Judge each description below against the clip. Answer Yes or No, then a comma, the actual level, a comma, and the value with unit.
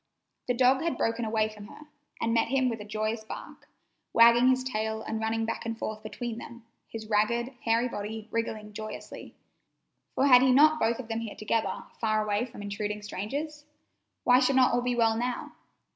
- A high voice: Yes, high, 230 Hz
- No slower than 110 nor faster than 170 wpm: No, average, 190 wpm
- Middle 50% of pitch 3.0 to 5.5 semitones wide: No, narrow, 2.4 semitones